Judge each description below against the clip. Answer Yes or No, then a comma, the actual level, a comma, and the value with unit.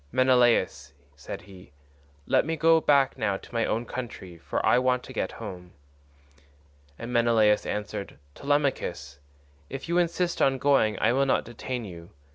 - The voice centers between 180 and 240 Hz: No, low, 120 Hz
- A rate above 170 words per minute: No, average, 155 wpm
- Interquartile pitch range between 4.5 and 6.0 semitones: Yes, average, 5.1 semitones